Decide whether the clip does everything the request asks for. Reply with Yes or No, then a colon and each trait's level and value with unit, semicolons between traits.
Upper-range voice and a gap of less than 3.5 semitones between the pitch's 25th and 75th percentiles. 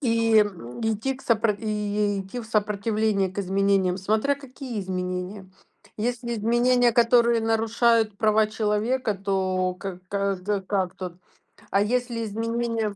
Yes: high, 215 Hz; average, 2.8 semitones